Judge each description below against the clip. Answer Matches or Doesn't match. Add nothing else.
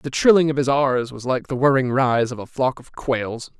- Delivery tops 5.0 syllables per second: Doesn't match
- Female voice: Doesn't match